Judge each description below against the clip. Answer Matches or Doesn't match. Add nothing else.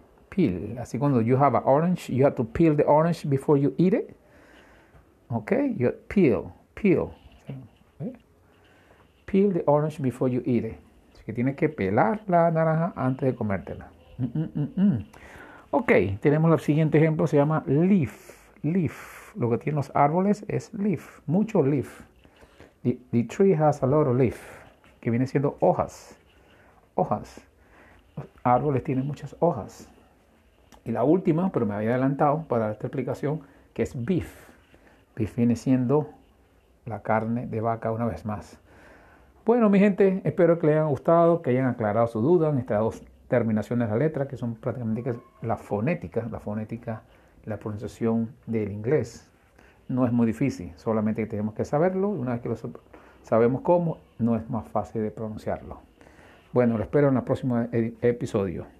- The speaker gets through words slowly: Doesn't match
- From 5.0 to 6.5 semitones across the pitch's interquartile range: Matches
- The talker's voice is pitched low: Matches